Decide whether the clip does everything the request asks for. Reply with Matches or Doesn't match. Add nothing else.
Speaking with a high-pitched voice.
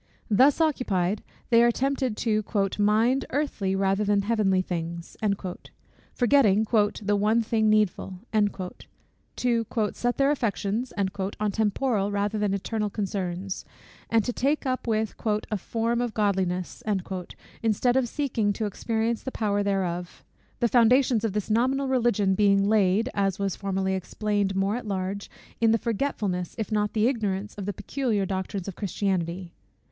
Matches